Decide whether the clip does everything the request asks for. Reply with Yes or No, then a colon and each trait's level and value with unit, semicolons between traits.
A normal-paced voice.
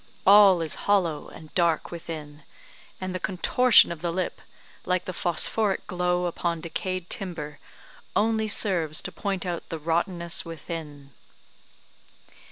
No: slow, 130 wpm